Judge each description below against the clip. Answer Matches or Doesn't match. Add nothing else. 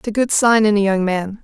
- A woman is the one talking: Matches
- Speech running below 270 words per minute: Doesn't match